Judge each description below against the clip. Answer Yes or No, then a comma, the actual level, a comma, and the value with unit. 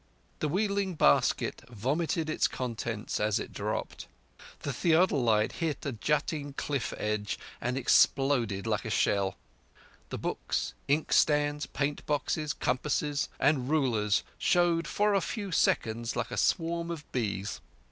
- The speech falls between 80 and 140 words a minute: Yes, slow, 135 wpm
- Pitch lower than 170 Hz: Yes, medium, 140 Hz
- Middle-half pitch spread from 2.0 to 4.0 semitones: No, wide, 5.5 semitones